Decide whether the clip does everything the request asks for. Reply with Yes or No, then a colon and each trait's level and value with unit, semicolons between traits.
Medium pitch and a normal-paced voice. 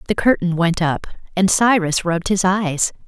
Yes: medium, 180 Hz; average, 175 wpm